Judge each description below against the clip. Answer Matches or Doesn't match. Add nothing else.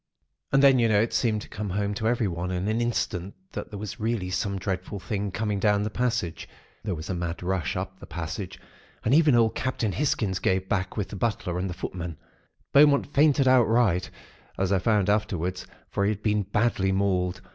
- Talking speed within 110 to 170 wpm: Doesn't match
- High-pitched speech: Doesn't match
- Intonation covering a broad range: Doesn't match